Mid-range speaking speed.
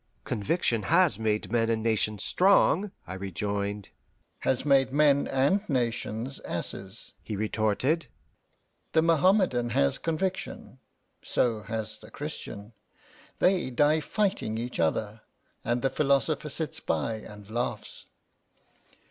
No: slow, 115 wpm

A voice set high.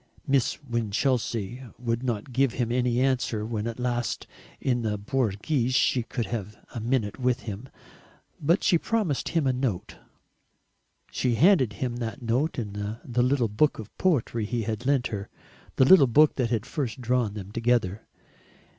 No: low, 120 Hz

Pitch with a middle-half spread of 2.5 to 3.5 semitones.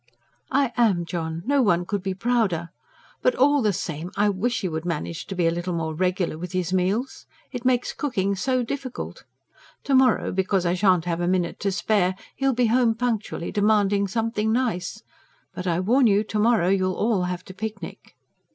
No: average, 4.7 semitones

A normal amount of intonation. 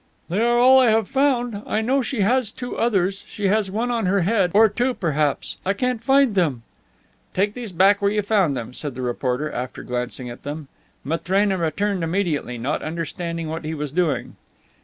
No: wide, 6.2 semitones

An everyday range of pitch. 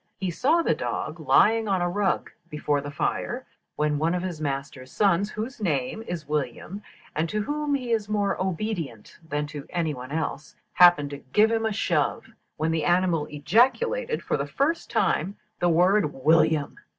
No: wide, 6.1 semitones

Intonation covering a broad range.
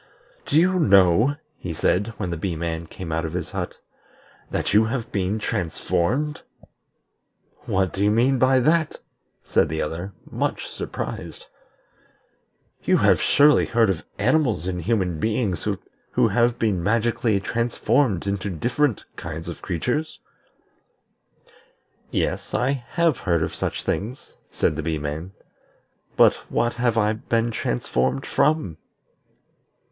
Yes: wide, 6.1 semitones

